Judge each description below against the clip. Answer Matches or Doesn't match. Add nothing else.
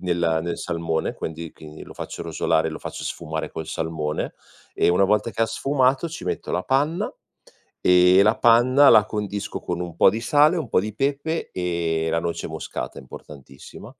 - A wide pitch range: Matches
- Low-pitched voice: Matches